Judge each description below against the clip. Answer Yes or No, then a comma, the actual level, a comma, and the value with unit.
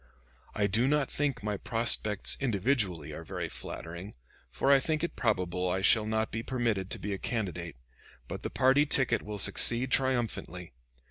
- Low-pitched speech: Yes, low, 110 Hz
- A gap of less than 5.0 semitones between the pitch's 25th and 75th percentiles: No, average, 5.3 semitones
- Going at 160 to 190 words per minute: Yes, average, 170 wpm